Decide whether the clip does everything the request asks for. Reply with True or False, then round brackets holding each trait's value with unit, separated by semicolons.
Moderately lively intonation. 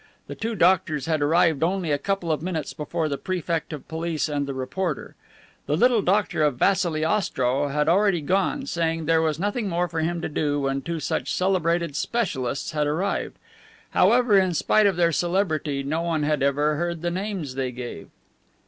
True (3.8 semitones)